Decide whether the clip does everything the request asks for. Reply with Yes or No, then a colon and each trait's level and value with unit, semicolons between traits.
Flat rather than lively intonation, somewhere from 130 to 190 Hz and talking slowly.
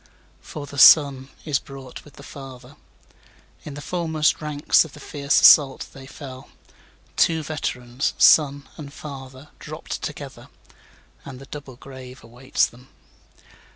Yes: narrow, 2.0 semitones; medium, 140 Hz; slow, 120 wpm